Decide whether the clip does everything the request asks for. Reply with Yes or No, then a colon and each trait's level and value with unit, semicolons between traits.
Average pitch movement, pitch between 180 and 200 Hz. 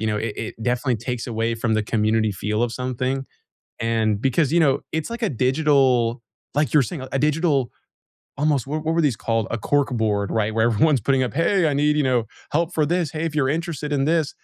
No: average, 5.0 semitones; low, 130 Hz